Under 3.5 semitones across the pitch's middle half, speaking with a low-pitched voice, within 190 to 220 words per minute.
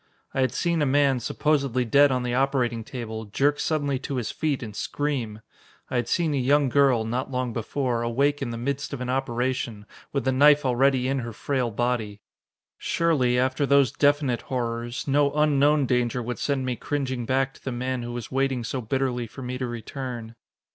Yes: average, 2.7 semitones; low, 130 Hz; average, 195 wpm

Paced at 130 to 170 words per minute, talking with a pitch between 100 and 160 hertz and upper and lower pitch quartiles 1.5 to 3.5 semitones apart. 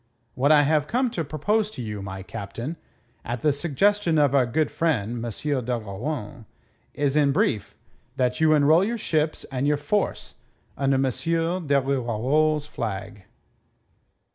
No: average, 145 wpm; medium, 140 Hz; average, 4.6 semitones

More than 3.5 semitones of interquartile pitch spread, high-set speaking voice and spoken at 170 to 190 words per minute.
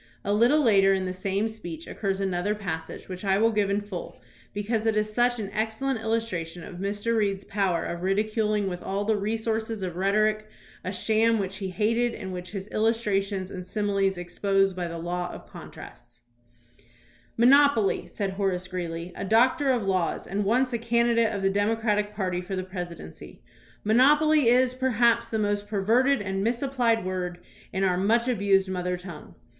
No: average, 3.2 semitones; high, 205 Hz; average, 180 wpm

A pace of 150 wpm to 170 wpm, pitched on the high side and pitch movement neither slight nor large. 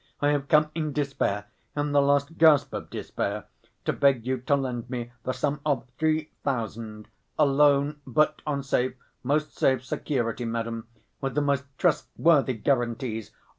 No: average, 160 wpm; medium, 140 Hz; average, 3.3 semitones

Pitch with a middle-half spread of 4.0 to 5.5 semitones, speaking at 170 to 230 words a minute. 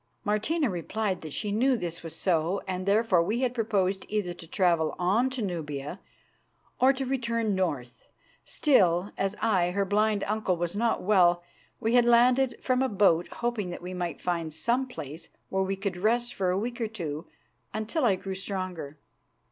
Yes: average, 4.6 semitones; average, 180 wpm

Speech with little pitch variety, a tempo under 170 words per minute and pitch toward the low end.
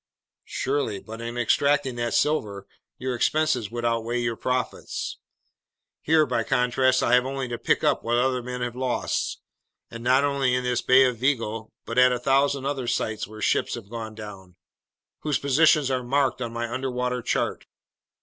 No: narrow, 2.3 semitones; average, 175 wpm; low, 125 Hz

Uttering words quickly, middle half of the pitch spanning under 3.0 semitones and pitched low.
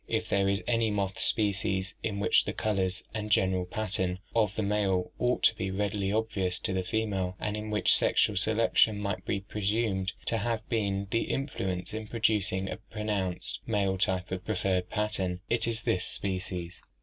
No: average, 175 wpm; narrow, 2.5 semitones; low, 100 Hz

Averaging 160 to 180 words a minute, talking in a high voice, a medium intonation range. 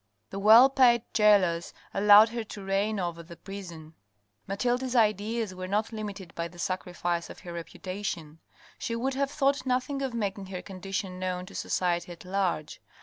Yes: average, 165 wpm; high, 195 Hz; average, 4.0 semitones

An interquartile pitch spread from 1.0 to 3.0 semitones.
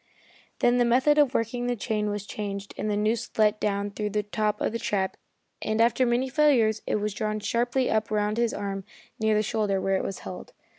Yes: narrow, 2.4 semitones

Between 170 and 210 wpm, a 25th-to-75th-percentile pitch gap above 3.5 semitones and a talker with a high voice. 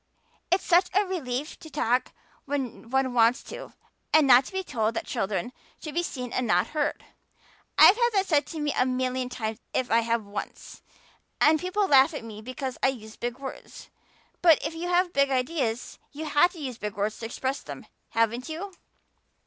Yes: average, 190 wpm; average, 5.1 semitones; very high, 265 Hz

